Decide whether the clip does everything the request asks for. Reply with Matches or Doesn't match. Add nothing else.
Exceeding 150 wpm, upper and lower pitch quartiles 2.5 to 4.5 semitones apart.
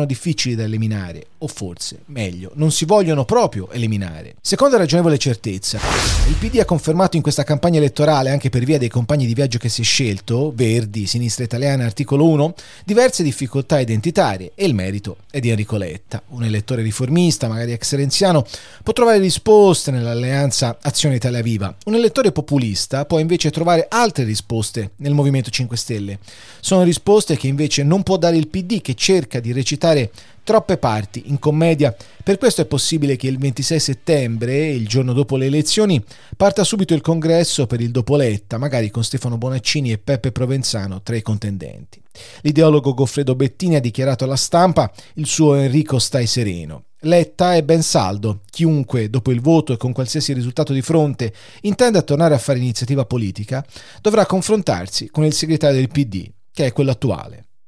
Doesn't match